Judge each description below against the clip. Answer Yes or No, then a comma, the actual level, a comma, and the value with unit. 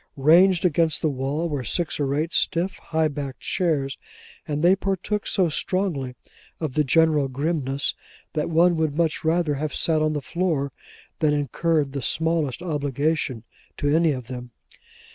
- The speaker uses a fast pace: No, average, 160 wpm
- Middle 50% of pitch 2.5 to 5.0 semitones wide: Yes, average, 3.1 semitones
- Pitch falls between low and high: Yes, medium, 155 Hz